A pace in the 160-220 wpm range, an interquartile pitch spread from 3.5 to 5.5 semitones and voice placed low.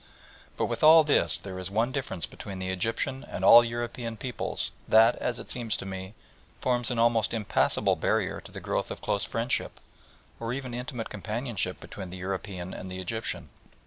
Yes: average, 180 wpm; average, 4.2 semitones; low, 115 Hz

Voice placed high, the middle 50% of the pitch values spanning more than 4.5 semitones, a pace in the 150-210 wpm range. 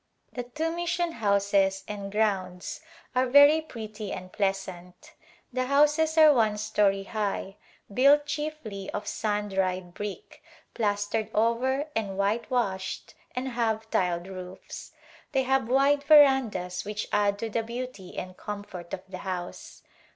No: high, 215 Hz; average, 5.1 semitones; slow, 135 wpm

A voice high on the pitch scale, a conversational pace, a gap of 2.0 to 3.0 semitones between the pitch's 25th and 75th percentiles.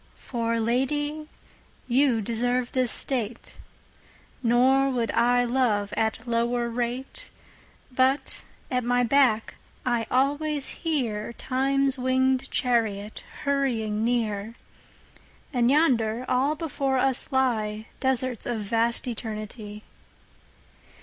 No: high, 245 Hz; slow, 85 wpm; narrow, 2.6 semitones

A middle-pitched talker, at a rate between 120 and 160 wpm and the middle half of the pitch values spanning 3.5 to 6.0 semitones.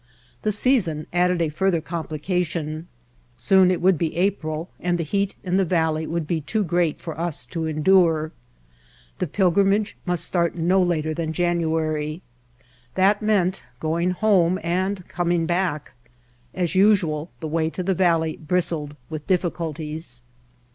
No: medium, 170 Hz; average, 145 wpm; average, 2.7 semitones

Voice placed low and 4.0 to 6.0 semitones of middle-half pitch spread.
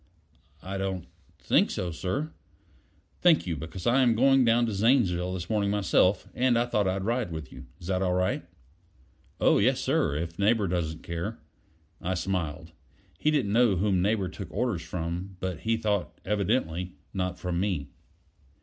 Yes: very low, 95 Hz; average, 4.4 semitones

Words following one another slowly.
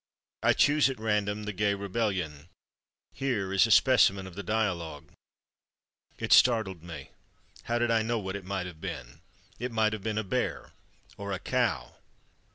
No: average, 165 wpm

